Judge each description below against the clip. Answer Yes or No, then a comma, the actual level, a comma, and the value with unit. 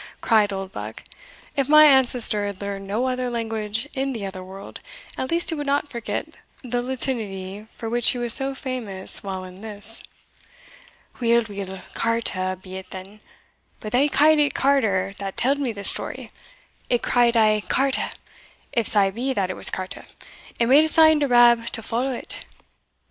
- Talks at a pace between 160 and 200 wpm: Yes, average, 175 wpm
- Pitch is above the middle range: Yes, high, 230 Hz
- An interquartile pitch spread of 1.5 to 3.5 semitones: No, average, 4.8 semitones